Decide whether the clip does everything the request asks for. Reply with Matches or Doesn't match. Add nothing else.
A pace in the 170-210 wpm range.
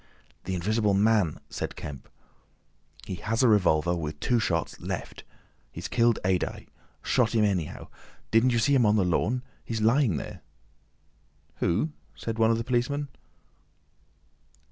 Doesn't match